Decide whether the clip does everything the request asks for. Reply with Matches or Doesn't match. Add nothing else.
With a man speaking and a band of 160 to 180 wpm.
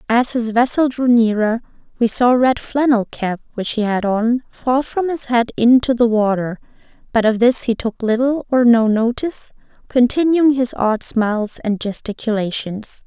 Doesn't match